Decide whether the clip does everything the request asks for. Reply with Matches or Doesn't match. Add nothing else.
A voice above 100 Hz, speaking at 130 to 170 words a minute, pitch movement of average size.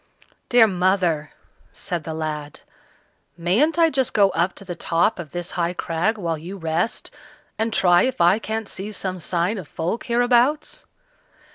Matches